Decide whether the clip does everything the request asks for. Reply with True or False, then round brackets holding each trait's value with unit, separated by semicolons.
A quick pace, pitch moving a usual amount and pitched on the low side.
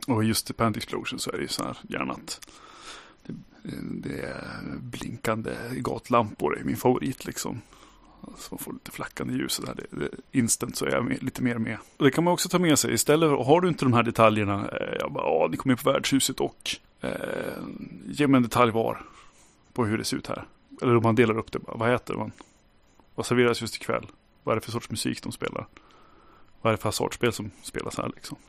True (220 wpm; 3.1 semitones; 120 Hz)